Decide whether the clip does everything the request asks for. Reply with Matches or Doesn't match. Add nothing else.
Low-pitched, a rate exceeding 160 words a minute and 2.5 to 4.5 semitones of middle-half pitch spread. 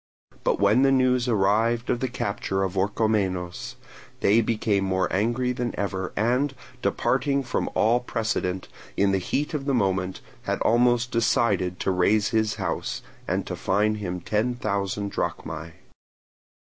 Doesn't match